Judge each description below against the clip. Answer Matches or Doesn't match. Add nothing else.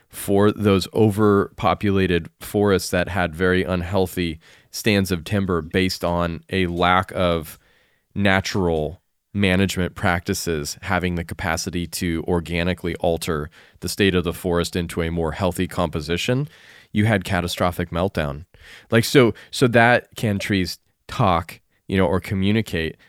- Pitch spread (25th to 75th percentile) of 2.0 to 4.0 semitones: Matches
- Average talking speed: Doesn't match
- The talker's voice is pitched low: Matches